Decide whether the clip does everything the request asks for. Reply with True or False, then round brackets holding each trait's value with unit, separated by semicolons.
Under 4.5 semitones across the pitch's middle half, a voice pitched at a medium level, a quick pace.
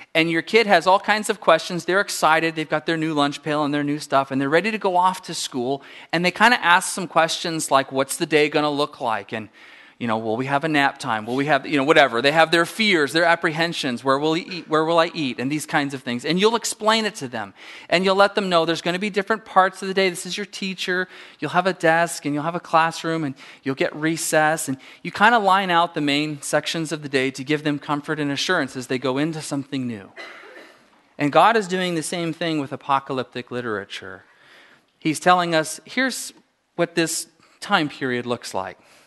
True (4.1 semitones; 160 Hz; 245 wpm)